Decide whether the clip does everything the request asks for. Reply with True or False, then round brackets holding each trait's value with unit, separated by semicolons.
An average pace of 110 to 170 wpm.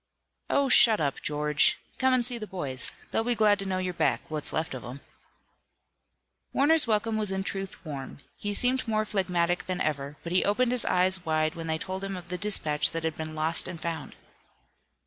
False (205 wpm)